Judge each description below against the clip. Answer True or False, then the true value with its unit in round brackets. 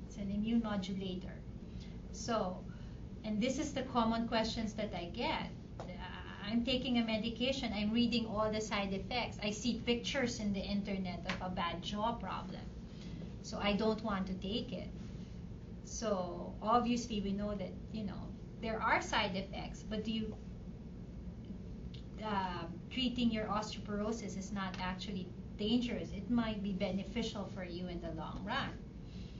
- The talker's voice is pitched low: False (210 Hz)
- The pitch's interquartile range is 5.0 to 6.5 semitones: False (3.0 semitones)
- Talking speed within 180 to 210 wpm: False (150 wpm)